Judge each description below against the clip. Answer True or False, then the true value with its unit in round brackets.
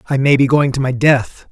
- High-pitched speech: False (135 Hz)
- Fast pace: True (280 wpm)